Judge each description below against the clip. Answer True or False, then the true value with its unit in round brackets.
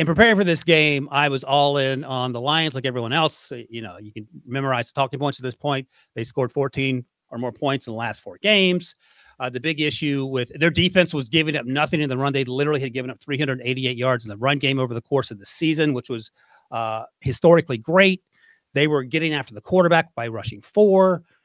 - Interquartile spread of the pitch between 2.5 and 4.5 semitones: True (4.0 semitones)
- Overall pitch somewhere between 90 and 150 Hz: True (140 Hz)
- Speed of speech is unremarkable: False (230 wpm)